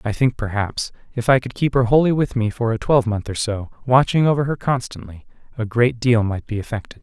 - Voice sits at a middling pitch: No, low, 120 Hz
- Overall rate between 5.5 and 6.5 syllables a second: Yes, 5.7 syllables/s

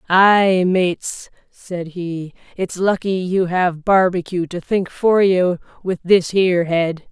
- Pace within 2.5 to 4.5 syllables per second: Yes, 3.5 syllables/s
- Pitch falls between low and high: Yes, medium, 180 Hz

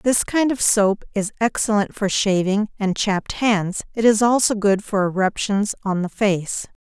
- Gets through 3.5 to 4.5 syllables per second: Yes, 4.4 syllables/s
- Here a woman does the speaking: Yes, female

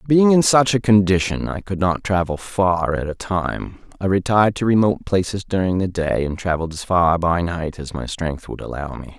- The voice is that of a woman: No, male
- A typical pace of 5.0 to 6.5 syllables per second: Yes, 5.1 syllables/s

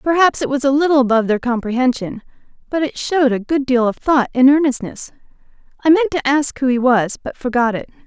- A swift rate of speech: Yes, fast, 210 wpm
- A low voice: No, very high, 265 Hz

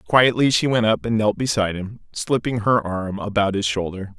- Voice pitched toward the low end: Yes, low, 110 Hz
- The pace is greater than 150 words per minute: Yes, average, 200 wpm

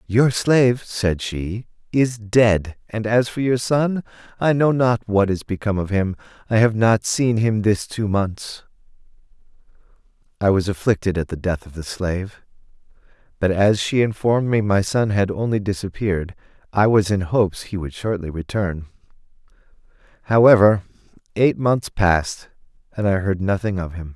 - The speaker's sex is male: Yes, male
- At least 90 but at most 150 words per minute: No, average, 160 wpm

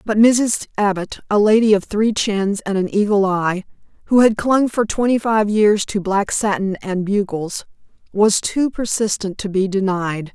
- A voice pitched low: No, high, 205 Hz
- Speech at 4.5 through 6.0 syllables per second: No, 4.3 syllables/s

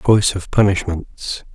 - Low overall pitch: Yes, very low, 95 Hz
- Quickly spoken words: No, slow, 115 wpm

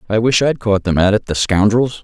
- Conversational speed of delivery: No, fast, 265 wpm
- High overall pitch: No, low, 110 Hz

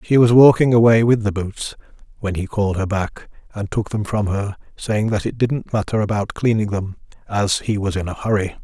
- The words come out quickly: Yes, fast, 215 wpm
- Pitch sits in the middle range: No, low, 105 Hz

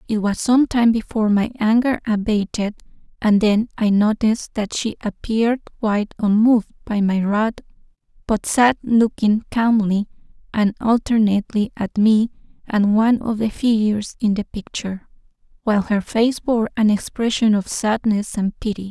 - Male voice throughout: No, female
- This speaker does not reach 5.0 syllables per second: Yes, 4.8 syllables/s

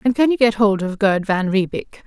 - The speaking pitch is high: Yes, high, 210 Hz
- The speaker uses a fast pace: Yes, fast, 260 wpm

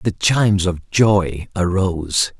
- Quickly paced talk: No, slow, 125 wpm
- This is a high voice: No, very low, 95 Hz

